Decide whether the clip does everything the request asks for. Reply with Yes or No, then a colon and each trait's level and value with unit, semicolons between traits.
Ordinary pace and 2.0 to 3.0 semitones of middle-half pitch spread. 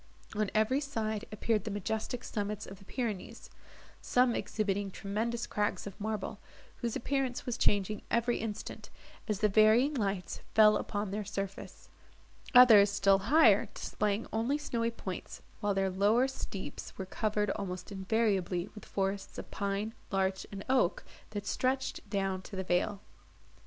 Yes: average, 145 wpm; average, 2.7 semitones